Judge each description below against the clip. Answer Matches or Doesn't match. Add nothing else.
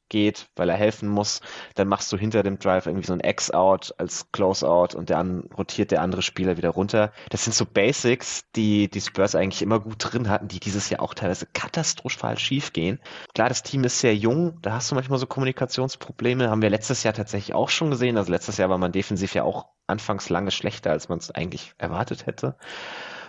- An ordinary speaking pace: Doesn't match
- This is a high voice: Doesn't match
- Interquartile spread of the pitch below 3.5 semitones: Doesn't match